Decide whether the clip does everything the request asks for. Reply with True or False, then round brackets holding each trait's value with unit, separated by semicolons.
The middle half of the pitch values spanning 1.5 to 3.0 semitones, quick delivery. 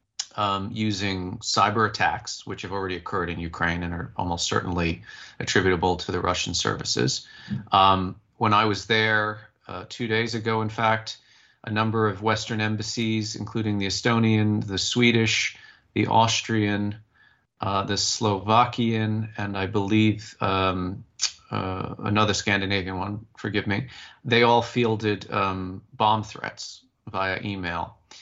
False (2.6 semitones; 135 wpm)